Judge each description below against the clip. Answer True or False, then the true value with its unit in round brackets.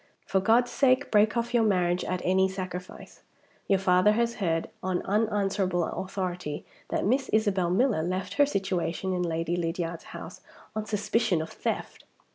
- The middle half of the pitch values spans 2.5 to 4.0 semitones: True (3.3 semitones)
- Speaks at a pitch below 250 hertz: True (190 Hz)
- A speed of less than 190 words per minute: True (155 wpm)